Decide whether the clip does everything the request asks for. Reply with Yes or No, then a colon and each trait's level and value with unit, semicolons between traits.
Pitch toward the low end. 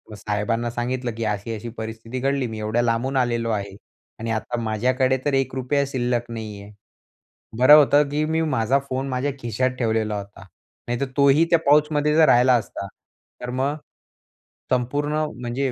Yes: low, 125 Hz